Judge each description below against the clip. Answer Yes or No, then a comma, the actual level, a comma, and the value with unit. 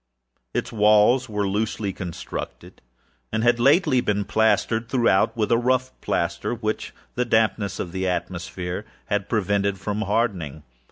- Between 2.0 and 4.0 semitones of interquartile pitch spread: Yes, average, 3.5 semitones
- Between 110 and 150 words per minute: Yes, slow, 135 wpm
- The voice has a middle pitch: No, low, 105 Hz